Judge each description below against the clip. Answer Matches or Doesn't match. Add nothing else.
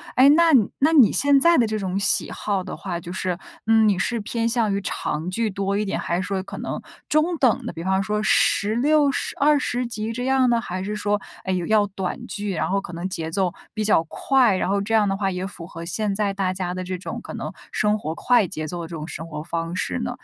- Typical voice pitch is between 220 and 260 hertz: Doesn't match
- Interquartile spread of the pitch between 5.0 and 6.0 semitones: Doesn't match